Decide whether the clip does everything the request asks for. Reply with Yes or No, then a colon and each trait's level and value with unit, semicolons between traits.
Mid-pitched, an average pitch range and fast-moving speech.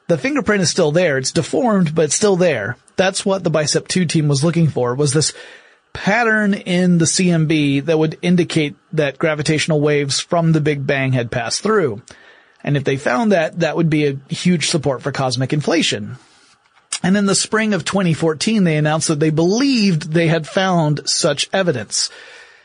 No: medium, 165 Hz; average, 3.8 semitones; average, 185 wpm